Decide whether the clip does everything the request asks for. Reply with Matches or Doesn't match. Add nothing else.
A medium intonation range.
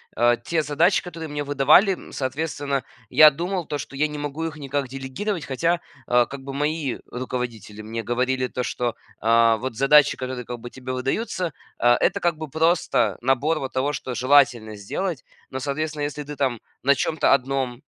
Matches